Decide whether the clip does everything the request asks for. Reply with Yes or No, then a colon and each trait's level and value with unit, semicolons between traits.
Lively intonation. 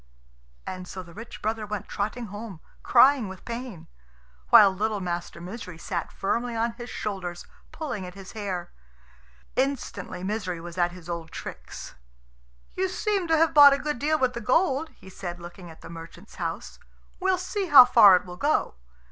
Yes: wide, 6.2 semitones